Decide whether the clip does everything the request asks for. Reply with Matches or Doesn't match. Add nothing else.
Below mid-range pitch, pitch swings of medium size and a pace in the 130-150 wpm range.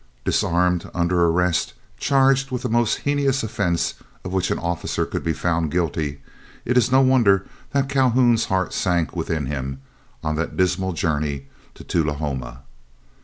Doesn't match